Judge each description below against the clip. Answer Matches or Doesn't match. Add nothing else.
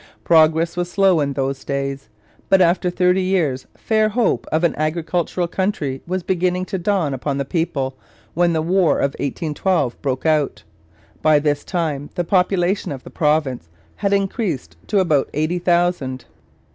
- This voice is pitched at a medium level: Matches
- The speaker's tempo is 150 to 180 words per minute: Matches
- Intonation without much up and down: Doesn't match